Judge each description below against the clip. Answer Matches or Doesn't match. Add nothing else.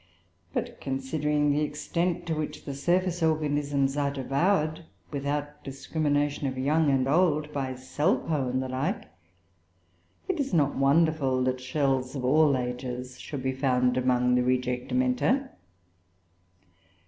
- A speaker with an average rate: Doesn't match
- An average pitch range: Matches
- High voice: Doesn't match